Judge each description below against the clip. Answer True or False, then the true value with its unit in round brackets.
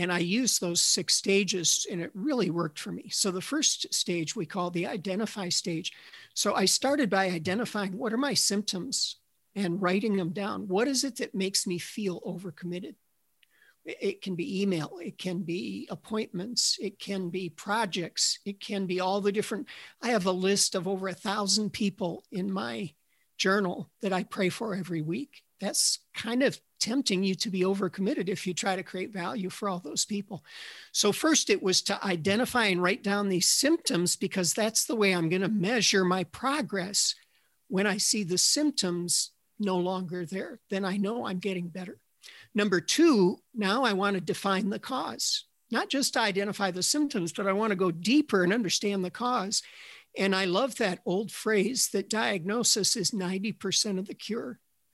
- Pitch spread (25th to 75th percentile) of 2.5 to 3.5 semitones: True (3.0 semitones)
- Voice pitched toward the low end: False (195 Hz)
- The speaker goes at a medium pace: True (185 wpm)